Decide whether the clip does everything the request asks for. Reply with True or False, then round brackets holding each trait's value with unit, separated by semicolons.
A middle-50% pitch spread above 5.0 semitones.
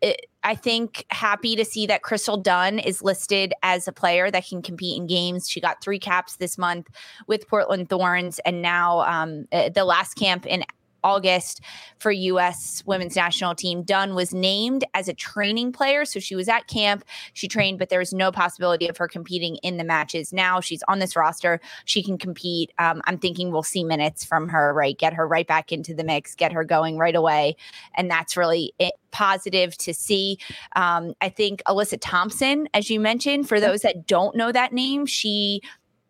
False (3.1 semitones)